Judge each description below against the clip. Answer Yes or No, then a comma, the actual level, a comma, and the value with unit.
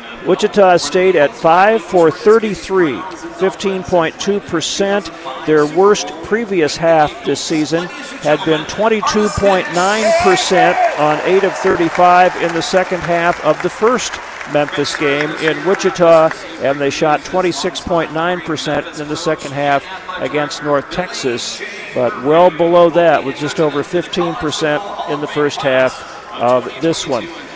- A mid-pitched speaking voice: Yes, medium, 170 Hz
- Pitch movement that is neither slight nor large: Yes, average, 3.8 semitones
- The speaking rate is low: Yes, slow, 125 wpm